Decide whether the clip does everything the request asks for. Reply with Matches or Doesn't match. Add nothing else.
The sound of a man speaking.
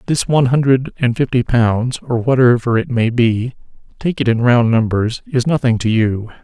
Matches